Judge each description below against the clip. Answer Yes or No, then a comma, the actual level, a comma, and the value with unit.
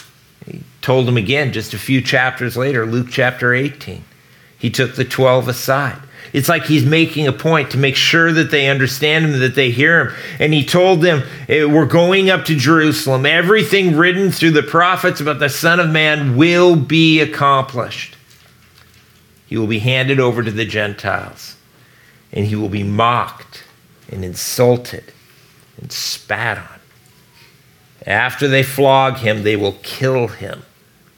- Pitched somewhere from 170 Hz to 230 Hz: No, low, 135 Hz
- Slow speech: No, average, 155 wpm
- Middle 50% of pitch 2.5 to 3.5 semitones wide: No, average, 4.1 semitones